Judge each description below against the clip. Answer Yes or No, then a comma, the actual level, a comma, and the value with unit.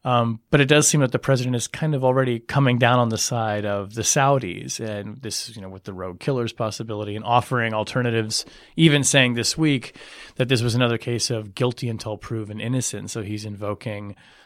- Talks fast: Yes, fast, 210 wpm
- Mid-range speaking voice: No, low, 115 Hz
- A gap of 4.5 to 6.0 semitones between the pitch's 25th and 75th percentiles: No, average, 3.2 semitones